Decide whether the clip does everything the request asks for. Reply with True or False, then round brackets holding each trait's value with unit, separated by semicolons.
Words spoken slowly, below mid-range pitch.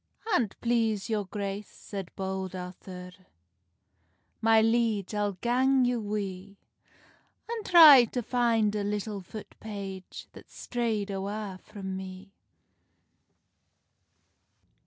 False (105 wpm; 210 Hz)